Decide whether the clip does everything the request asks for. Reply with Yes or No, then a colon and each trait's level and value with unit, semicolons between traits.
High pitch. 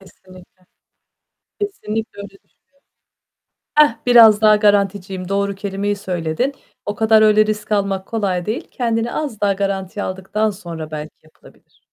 Yes: high, 200 Hz